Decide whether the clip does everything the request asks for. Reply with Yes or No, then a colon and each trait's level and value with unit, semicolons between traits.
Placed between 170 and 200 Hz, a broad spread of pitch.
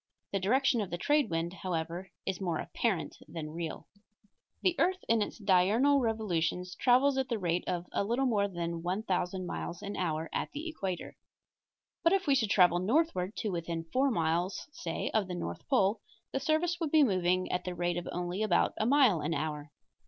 Yes: high, 190 Hz; wide, 6.1 semitones